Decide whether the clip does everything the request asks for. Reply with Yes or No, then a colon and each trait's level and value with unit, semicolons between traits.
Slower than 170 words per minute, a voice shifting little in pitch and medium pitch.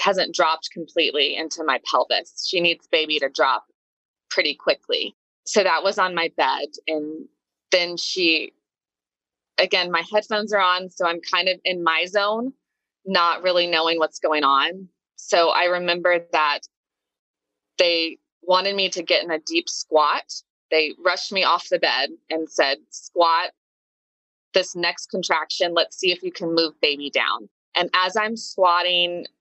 Yes: average, 155 wpm; narrow, 2.2 semitones; medium, 175 Hz